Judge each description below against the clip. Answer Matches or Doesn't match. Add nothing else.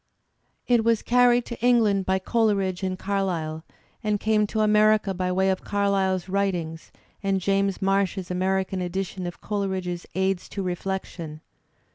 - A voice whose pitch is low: Doesn't match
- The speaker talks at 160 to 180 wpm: Doesn't match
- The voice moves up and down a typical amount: Doesn't match